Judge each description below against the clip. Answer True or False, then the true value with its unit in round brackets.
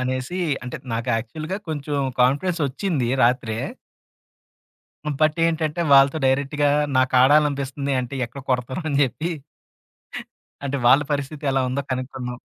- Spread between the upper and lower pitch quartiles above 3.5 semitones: False (2.8 semitones)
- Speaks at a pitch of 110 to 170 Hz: True (140 Hz)